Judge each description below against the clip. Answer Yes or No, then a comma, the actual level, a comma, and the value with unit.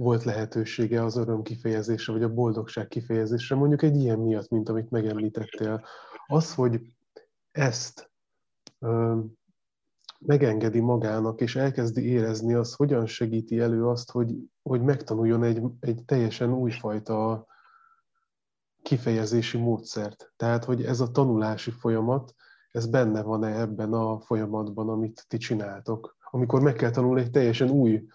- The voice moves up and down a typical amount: No, narrow, 2.1 semitones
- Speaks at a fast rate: No, average, 130 wpm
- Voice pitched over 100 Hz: Yes, low, 115 Hz